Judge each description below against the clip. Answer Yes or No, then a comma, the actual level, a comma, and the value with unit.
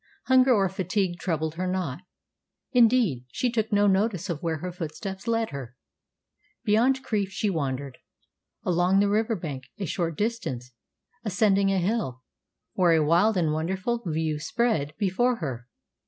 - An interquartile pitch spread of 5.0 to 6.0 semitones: Yes, wide, 5.4 semitones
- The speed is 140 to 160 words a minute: Yes, average, 150 wpm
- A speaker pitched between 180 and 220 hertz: Yes, medium, 185 Hz